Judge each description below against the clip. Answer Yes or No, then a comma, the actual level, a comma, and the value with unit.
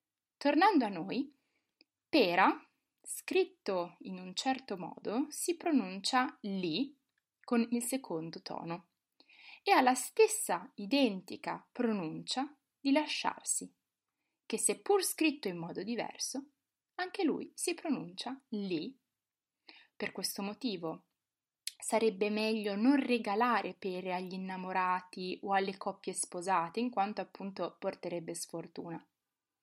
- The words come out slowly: Yes, slow, 110 wpm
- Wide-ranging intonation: Yes, wide, 6.7 semitones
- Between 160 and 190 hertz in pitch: No, high, 220 Hz